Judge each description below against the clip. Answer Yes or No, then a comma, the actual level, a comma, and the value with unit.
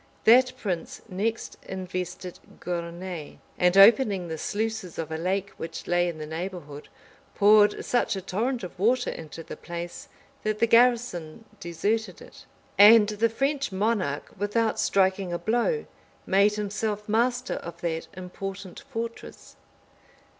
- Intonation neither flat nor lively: Yes, average, 4.4 semitones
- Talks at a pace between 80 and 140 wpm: Yes, slow, 135 wpm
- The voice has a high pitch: Yes, high, 200 Hz